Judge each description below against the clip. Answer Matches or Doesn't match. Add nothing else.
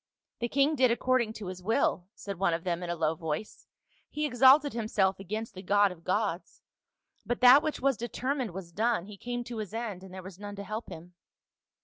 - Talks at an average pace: Doesn't match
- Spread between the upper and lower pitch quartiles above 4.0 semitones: Matches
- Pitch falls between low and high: Doesn't match